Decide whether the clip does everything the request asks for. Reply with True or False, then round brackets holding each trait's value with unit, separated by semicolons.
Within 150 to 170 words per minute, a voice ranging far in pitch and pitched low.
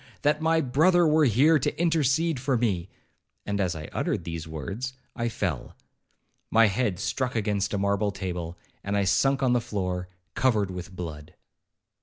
True (160 wpm; 6.7 semitones; 105 Hz)